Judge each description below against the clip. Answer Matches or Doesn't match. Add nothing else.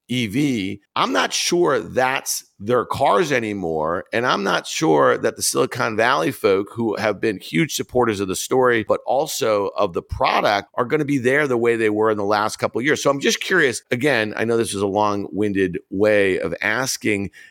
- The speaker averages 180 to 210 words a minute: Matches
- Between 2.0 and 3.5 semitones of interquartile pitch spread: Doesn't match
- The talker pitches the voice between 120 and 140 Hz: Doesn't match